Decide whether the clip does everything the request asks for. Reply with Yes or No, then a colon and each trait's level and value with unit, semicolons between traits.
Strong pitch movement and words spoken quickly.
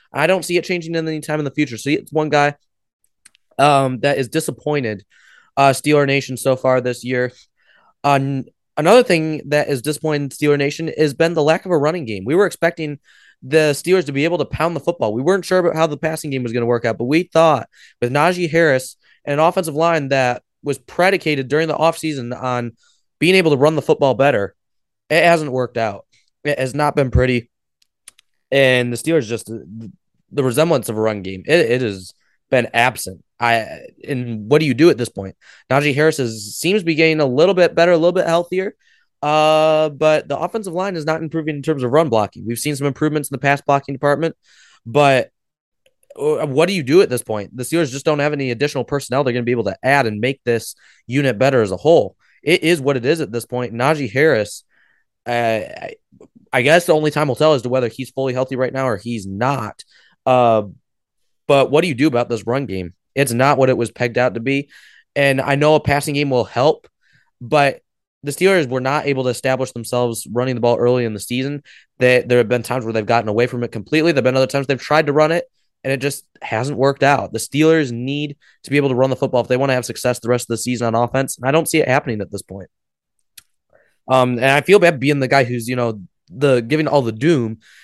No: average, 4.0 semitones; fast, 230 wpm